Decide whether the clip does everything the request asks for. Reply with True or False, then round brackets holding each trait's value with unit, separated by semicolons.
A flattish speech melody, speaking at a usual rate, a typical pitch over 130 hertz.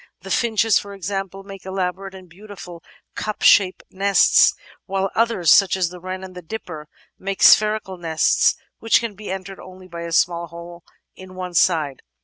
True (2.1 semitones; 170 wpm; 185 Hz)